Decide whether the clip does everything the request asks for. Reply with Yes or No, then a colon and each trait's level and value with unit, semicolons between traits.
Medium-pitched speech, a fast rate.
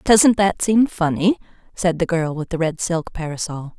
No: medium, 175 Hz; average, 190 wpm